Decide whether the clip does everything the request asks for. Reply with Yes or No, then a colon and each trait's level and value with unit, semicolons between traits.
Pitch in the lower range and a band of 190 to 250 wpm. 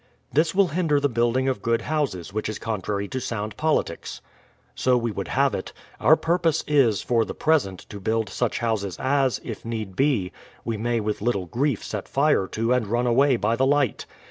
Yes: low, 120 Hz; average, 200 wpm